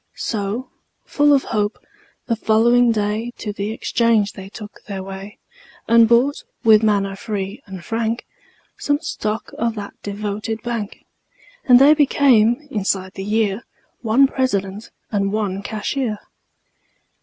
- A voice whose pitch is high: Yes, high, 220 Hz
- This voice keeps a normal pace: No, slow, 130 wpm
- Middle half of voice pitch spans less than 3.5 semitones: Yes, average, 2.8 semitones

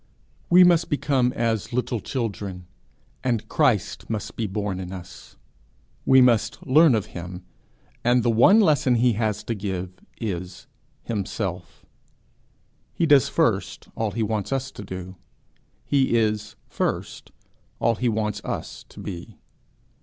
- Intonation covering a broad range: No, average, 4.6 semitones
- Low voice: Yes, low, 110 Hz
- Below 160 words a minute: Yes, average, 140 wpm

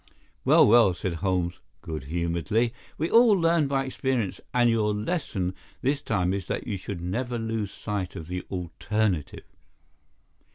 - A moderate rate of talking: Yes, average, 150 wpm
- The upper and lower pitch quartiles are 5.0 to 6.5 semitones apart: Yes, average, 5.3 semitones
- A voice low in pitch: Yes, low, 105 Hz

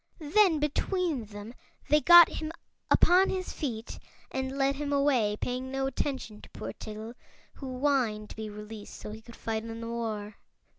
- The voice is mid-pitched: No, very high, 255 Hz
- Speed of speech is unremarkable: Yes, average, 170 wpm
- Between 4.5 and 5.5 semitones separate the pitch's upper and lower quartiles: Yes, average, 4.9 semitones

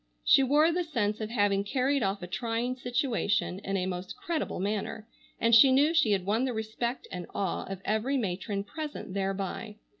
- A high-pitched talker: Yes, high, 220 Hz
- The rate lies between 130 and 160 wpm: No, average, 185 wpm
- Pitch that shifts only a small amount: No, average, 4.6 semitones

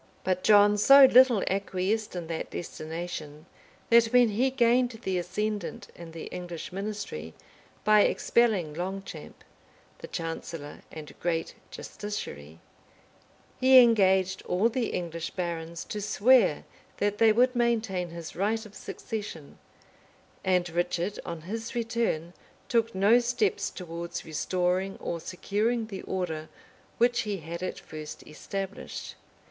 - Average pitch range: Yes, average, 4.8 semitones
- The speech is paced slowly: Yes, slow, 130 wpm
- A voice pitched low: No, high, 190 Hz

